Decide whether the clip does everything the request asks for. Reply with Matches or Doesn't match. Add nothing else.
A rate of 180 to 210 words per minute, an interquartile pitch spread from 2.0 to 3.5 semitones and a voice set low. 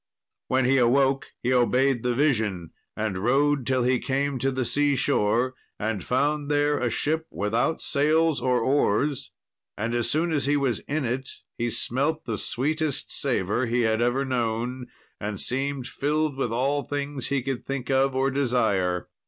Doesn't match